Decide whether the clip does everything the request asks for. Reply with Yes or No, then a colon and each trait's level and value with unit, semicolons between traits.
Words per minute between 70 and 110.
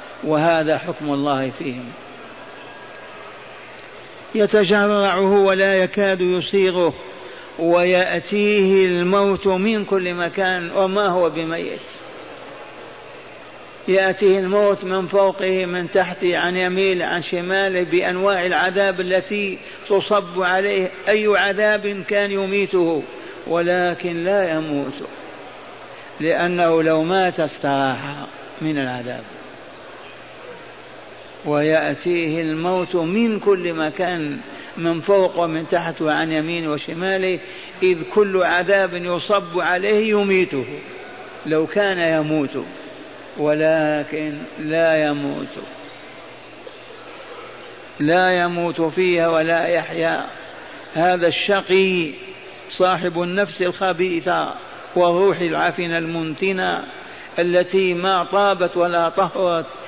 Yes: average, 85 wpm